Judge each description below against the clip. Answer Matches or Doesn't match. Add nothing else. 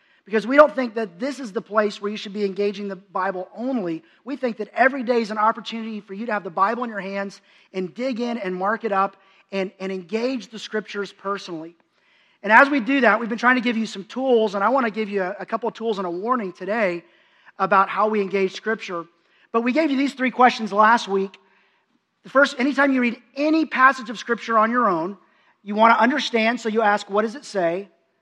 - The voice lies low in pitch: Doesn't match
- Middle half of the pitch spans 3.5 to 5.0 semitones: Matches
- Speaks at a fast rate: Matches